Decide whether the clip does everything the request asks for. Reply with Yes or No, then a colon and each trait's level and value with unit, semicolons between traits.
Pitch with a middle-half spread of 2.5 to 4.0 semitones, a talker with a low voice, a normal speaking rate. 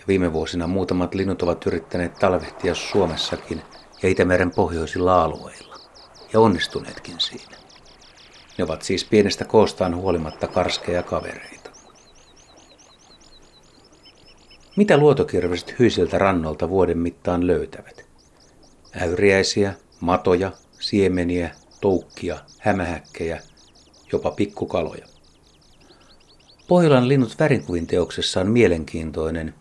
No: average, 2.9 semitones; very low, 90 Hz; slow, 85 wpm